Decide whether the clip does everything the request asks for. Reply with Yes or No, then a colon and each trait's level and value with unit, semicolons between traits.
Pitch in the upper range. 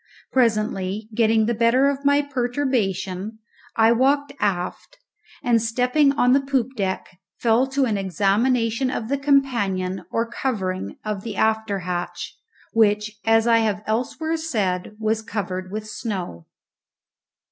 Yes: high, 225 Hz